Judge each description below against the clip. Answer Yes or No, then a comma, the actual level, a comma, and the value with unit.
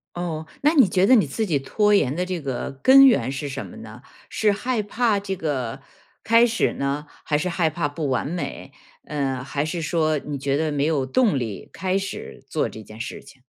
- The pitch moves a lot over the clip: Yes, wide, 6.3 semitones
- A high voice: No, medium, 155 Hz